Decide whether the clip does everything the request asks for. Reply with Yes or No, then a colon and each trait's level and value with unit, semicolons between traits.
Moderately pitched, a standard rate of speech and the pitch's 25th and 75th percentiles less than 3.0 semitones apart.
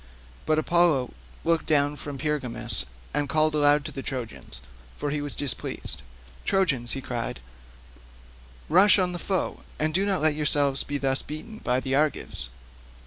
Yes: medium, 150 Hz; average, 155 wpm; narrow, 2.6 semitones